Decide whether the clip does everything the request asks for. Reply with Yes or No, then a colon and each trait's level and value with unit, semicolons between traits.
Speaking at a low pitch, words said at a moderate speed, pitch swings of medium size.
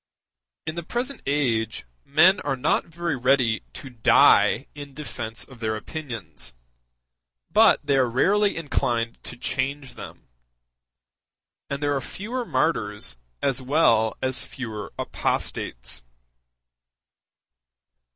No: low, 130 Hz; slow, 110 wpm; average, 4.9 semitones